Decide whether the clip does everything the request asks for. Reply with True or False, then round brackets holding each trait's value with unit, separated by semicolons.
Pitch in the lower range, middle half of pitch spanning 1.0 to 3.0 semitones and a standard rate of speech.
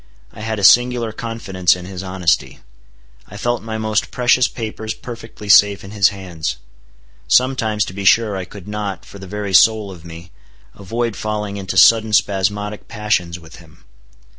True (105 Hz; 2.7 semitones; 165 wpm)